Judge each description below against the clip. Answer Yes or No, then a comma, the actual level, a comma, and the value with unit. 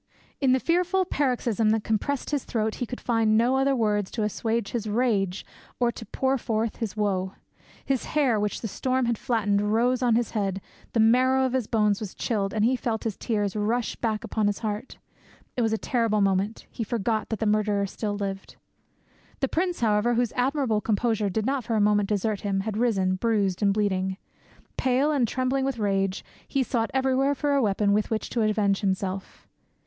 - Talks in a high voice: Yes, high, 220 Hz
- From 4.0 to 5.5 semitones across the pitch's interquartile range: No, average, 3.3 semitones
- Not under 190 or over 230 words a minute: Yes, average, 195 wpm